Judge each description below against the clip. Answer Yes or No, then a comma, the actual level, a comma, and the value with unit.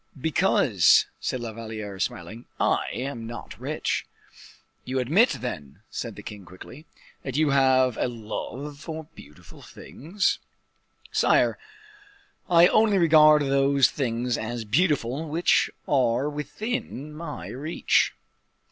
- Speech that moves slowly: Yes, slow, 120 wpm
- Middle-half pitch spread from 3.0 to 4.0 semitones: No, average, 4.8 semitones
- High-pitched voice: No, low, 135 Hz